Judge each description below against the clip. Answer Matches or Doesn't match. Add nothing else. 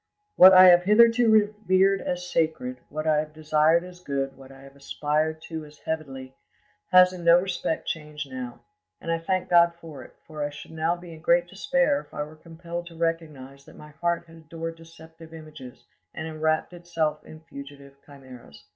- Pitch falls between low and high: Matches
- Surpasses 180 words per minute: Matches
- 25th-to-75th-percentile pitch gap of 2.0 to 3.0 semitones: Matches